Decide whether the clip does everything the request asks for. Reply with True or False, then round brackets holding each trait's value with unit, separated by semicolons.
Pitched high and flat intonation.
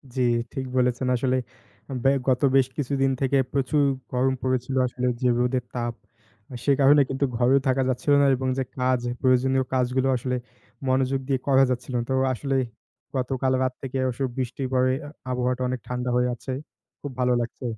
False (130 Hz; 1.1 semitones)